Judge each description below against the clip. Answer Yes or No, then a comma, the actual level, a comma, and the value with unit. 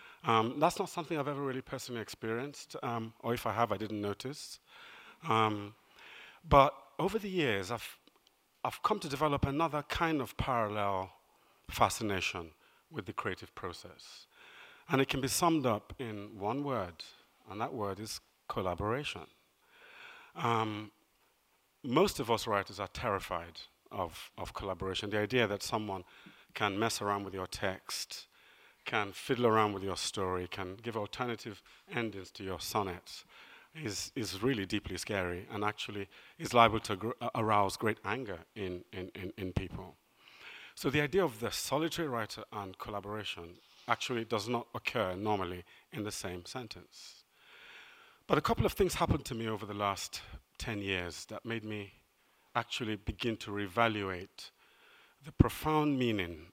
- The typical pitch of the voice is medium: No, low, 110 Hz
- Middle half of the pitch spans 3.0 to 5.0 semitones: Yes, average, 4.7 semitones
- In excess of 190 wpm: No, average, 150 wpm